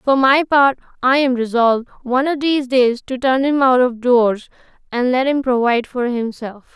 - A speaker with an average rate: Yes, average, 195 wpm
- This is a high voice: Yes, very high, 255 Hz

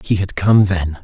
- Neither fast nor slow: No, fast, 230 wpm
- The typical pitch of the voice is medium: No, very low, 95 Hz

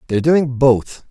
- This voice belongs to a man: Yes, male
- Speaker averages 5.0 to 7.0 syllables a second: No, 4.5 syllables/s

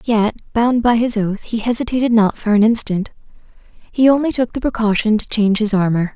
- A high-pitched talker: Yes, high, 220 Hz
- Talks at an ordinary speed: Yes, average, 195 wpm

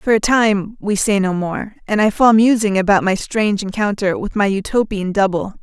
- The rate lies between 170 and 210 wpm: Yes, fast, 205 wpm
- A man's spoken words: No, female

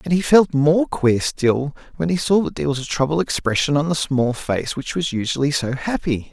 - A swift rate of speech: Yes, fast, 230 wpm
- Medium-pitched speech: Yes, medium, 145 Hz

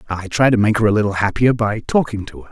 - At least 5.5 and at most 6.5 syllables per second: Yes, 6.4 syllables/s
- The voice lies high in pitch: No, low, 105 Hz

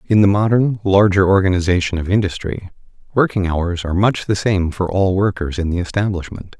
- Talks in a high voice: No, very low, 95 Hz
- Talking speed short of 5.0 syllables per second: No, 5.5 syllables/s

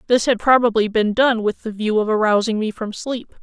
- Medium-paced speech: No, fast, 230 wpm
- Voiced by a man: No, female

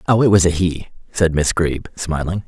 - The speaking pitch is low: Yes, very low, 85 Hz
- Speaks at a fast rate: Yes, fast, 220 wpm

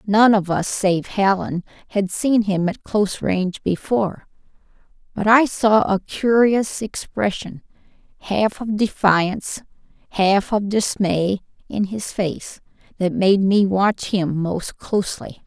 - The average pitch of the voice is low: No, high, 200 Hz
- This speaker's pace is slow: Yes, slow, 130 wpm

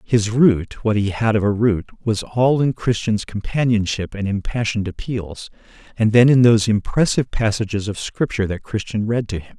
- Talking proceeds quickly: No, average, 180 wpm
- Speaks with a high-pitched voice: No, low, 110 Hz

